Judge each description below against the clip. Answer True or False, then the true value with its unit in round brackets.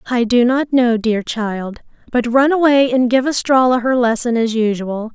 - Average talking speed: True (185 wpm)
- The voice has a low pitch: False (240 Hz)